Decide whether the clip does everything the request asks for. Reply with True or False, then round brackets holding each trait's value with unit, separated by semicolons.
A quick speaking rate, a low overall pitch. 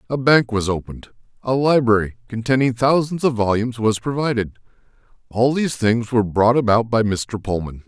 False (160 wpm; 115 Hz)